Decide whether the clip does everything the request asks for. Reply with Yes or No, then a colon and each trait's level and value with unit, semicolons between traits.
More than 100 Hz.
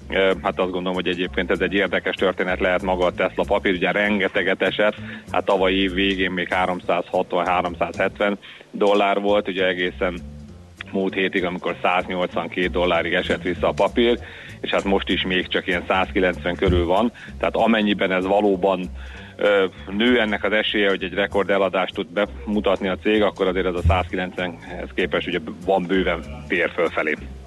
No: very low, 95 Hz